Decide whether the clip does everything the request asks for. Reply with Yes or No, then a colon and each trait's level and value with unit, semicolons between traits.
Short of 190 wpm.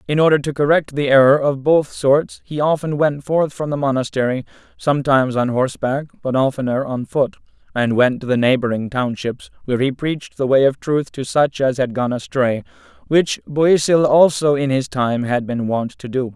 No: average, 195 wpm